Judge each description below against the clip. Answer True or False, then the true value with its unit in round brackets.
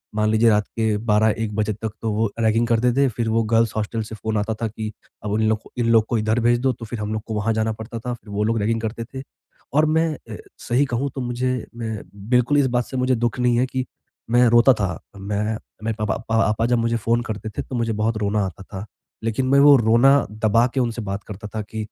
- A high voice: False (115 Hz)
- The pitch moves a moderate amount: False (2.0 semitones)